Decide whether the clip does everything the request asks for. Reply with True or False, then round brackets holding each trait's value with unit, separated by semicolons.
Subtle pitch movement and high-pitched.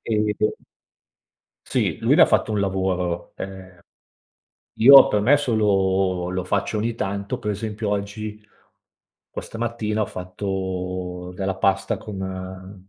False (2.3 semitones; 100 Hz)